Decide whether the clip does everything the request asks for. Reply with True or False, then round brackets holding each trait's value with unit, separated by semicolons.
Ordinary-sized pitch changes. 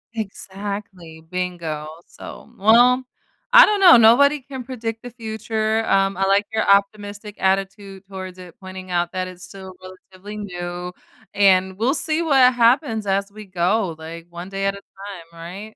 True (3.2 semitones)